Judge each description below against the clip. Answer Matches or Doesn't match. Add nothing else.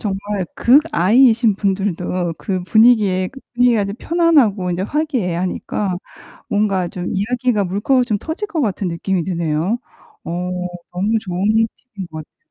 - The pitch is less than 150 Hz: Doesn't match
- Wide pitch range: Doesn't match